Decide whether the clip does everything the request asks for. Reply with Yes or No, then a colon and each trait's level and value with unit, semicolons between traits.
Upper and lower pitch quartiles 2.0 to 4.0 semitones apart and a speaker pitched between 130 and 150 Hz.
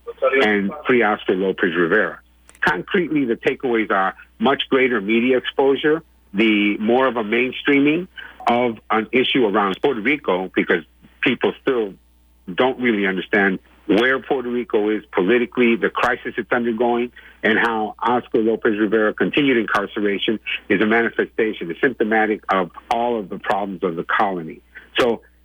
No: average, 2.8 semitones; low, 115 Hz